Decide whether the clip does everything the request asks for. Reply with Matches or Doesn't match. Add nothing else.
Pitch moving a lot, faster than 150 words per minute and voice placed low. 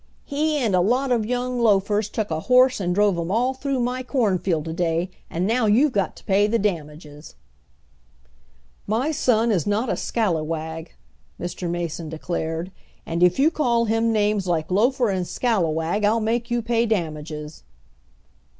Doesn't match